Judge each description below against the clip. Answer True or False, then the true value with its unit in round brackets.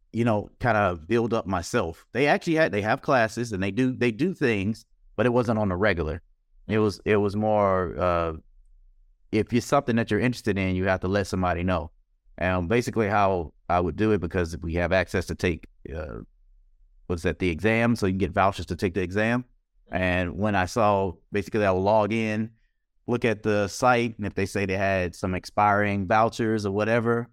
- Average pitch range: True (3.8 semitones)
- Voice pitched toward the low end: True (100 Hz)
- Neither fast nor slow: False (210 wpm)